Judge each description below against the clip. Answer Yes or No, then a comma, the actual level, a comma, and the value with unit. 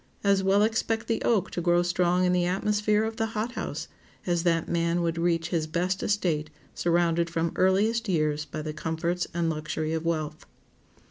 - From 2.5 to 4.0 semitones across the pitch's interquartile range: Yes, average, 3.3 semitones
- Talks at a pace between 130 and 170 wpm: No, average, 185 wpm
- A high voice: No, medium, 175 Hz